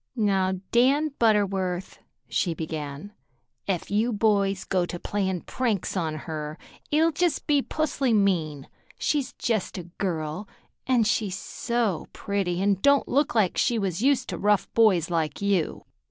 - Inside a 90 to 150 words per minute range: Yes, average, 145 wpm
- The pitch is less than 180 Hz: No, high, 200 Hz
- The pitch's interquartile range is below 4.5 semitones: No, average, 5.1 semitones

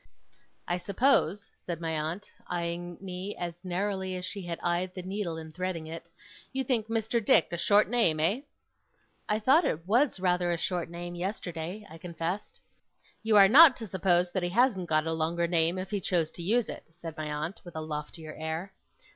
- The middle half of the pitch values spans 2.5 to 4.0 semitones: Yes, average, 3.5 semitones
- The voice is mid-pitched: Yes, medium, 180 Hz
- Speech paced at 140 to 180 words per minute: No, average, 195 wpm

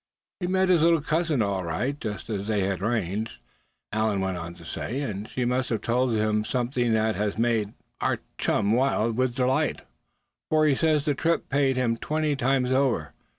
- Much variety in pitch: No, average, 4.5 semitones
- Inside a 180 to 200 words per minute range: Yes, average, 190 wpm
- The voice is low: Yes, low, 120 Hz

